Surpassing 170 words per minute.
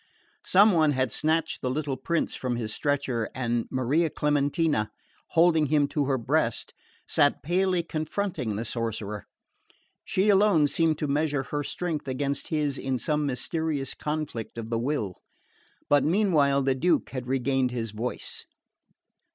No: average, 145 wpm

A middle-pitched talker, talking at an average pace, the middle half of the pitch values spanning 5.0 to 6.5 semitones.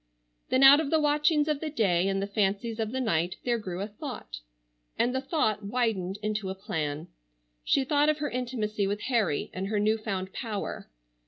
No: high, 215 Hz; average, 190 wpm; wide, 5.4 semitones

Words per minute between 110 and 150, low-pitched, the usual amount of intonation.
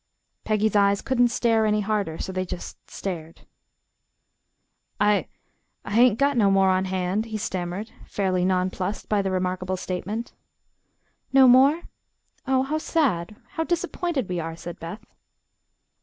No: average, 140 wpm; high, 205 Hz; average, 4.4 semitones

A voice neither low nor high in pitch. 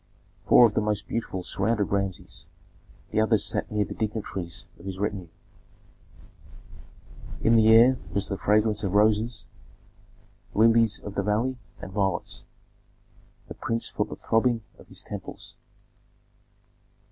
No: low, 105 Hz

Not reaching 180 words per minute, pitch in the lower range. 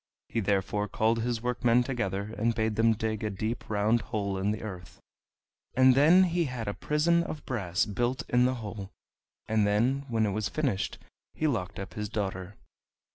No: average, 185 wpm; low, 110 Hz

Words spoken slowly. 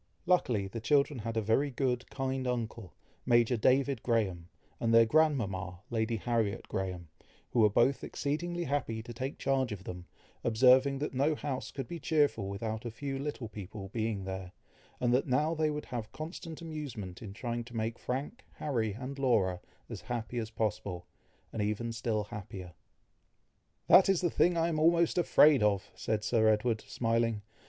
No: average, 170 wpm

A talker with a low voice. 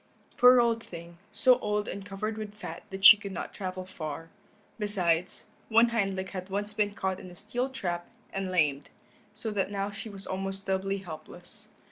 No: high, 195 Hz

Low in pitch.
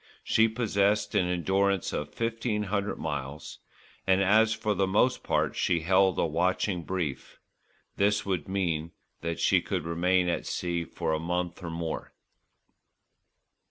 Yes: very low, 95 Hz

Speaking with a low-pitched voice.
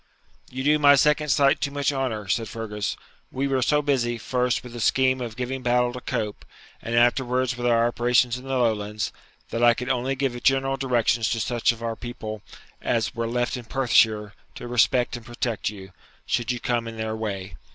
Yes: low, 120 Hz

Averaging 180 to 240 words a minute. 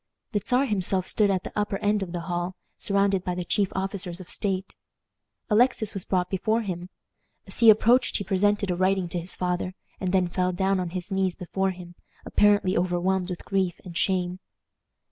Yes: average, 190 wpm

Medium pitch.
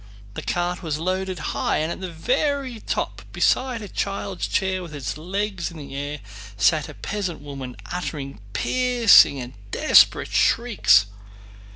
Yes: medium, 180 Hz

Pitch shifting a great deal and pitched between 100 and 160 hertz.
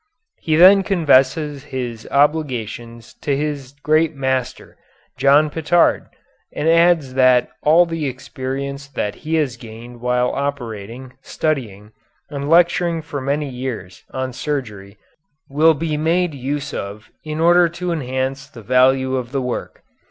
No: average, 3.7 semitones; medium, 140 Hz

